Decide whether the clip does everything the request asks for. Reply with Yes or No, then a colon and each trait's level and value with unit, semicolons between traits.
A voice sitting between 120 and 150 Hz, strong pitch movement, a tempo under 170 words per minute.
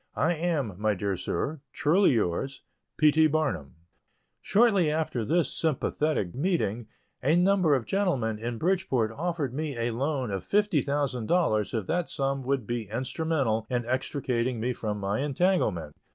Yes: low, 135 Hz; wide, 6.1 semitones; average, 145 wpm